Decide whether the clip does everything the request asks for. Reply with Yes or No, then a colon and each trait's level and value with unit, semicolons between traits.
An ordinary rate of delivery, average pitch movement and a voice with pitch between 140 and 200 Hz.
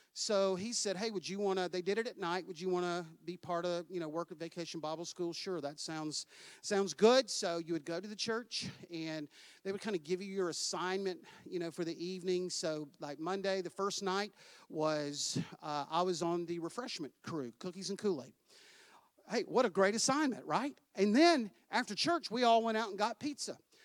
No: fast, 215 wpm; average, 3.4 semitones; medium, 185 Hz